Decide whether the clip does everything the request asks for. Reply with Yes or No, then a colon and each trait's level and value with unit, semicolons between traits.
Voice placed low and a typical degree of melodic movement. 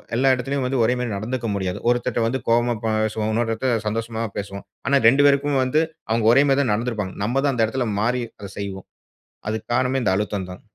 Yes: low, 115 Hz; average, 3.1 semitones